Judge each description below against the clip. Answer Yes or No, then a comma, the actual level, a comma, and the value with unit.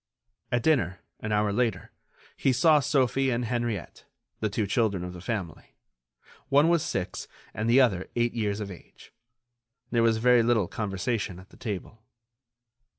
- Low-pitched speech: Yes, low, 115 Hz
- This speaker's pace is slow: No, average, 155 wpm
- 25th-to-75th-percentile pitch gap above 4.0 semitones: No, average, 3.7 semitones